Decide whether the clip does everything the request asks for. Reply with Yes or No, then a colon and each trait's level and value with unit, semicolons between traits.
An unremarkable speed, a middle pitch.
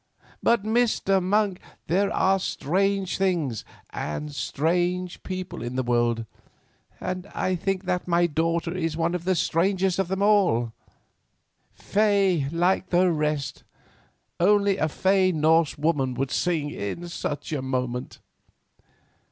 No: slow, 125 wpm; medium, 175 Hz